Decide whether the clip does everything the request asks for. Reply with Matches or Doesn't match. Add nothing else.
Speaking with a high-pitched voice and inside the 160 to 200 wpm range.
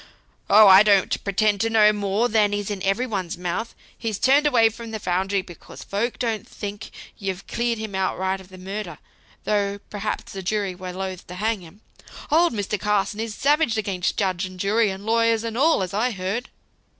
Matches